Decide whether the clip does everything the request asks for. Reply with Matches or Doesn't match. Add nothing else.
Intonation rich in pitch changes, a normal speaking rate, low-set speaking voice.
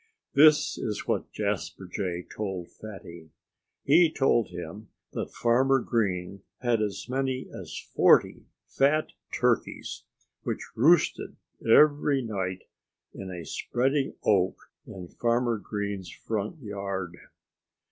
Doesn't match